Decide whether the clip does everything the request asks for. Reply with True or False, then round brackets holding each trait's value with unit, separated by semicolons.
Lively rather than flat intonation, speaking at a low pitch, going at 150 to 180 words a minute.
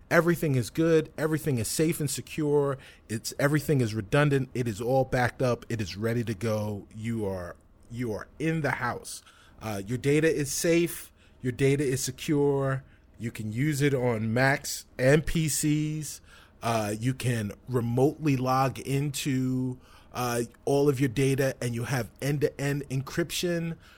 False (3.8 semitones; 130 Hz; 155 wpm)